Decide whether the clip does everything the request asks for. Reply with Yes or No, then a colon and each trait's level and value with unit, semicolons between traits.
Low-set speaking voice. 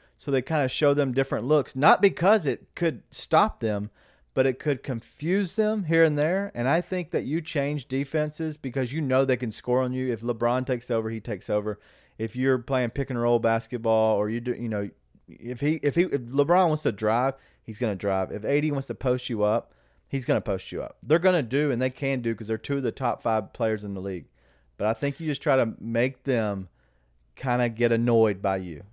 Yes: low, 125 Hz